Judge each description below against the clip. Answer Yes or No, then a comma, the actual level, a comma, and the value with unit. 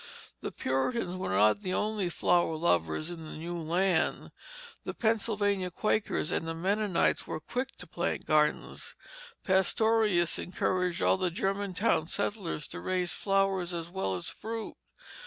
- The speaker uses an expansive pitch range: No, average, 3.5 semitones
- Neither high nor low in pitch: Yes, medium, 180 Hz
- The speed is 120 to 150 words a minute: Yes, average, 140 wpm